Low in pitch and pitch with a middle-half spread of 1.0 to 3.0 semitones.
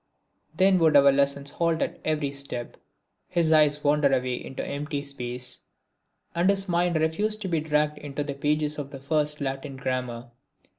No: medium, 150 Hz; narrow, 2.5 semitones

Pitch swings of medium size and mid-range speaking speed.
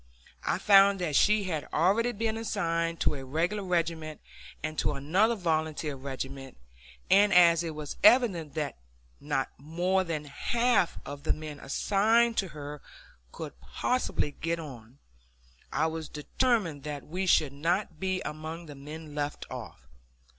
Yes: average, 4.6 semitones; average, 145 wpm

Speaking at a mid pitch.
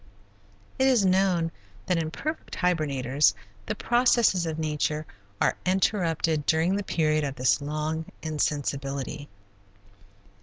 Yes: medium, 160 Hz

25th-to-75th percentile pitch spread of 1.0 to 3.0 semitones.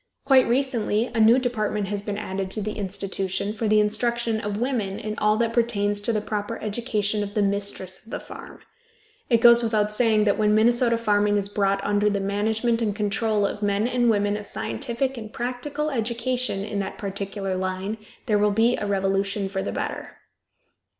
Yes: narrow, 2.4 semitones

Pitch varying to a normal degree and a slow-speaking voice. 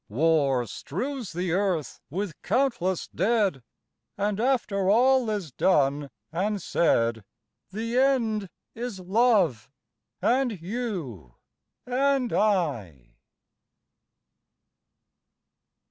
No: wide, 7.4 semitones; slow, 85 wpm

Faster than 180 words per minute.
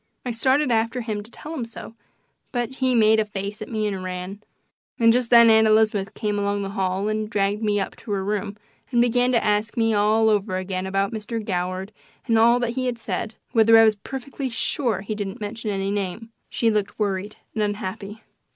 Yes: fast, 205 wpm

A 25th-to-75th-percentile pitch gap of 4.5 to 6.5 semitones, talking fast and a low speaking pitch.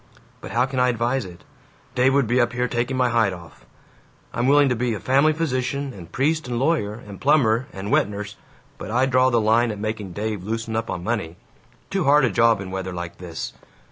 No: average, 4.0 semitones; fast, 215 wpm; low, 120 Hz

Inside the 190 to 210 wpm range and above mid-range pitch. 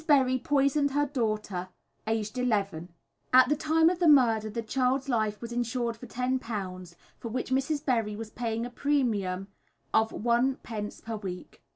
No: average, 160 wpm; high, 235 Hz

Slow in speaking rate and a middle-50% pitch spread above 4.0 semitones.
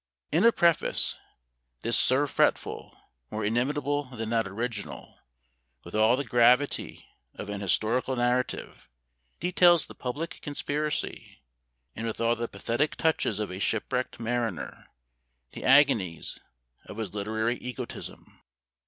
Yes: slow, 125 wpm; average, 4.6 semitones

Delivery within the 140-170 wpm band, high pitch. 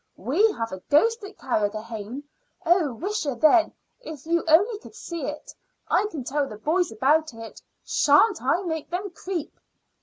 Yes: average, 160 wpm; very high, 310 Hz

